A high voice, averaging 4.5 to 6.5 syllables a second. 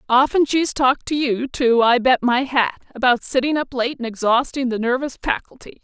Yes: very high, 255 Hz; 5.2 syllables/s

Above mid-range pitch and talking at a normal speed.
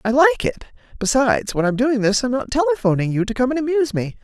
No: very high, 250 Hz; fast, 240 wpm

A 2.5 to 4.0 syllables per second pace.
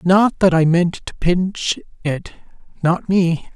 Yes: 3.4 syllables/s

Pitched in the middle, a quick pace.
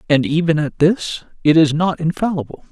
No: medium, 160 Hz; average, 175 wpm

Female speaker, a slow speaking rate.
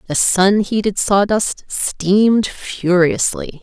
Yes: female; slow, 100 wpm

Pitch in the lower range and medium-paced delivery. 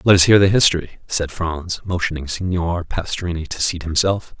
Yes: very low, 85 Hz; average, 175 wpm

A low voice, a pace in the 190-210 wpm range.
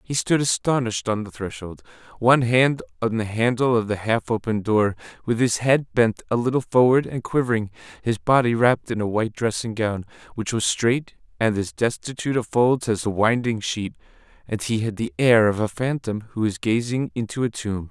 Yes: low, 115 Hz; average, 200 wpm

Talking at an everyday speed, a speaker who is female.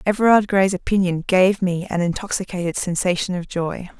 Yes: average, 150 wpm; female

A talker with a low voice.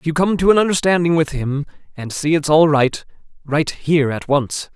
No: medium, 155 Hz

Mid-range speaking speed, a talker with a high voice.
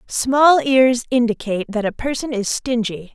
Yes: average, 155 wpm; high, 240 Hz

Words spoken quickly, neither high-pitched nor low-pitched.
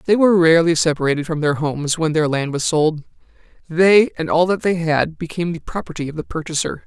Yes: fast, 210 wpm; medium, 160 Hz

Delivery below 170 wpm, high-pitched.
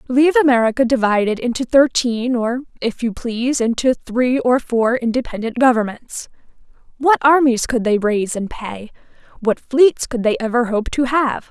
Yes: average, 145 wpm; high, 245 Hz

